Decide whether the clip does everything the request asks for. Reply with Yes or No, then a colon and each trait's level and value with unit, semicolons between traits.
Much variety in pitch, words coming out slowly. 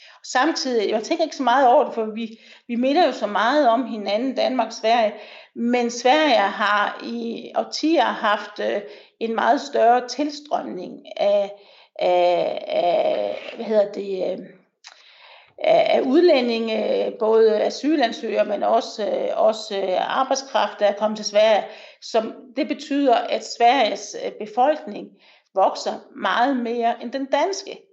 Yes: wide, 5.8 semitones; slow, 130 wpm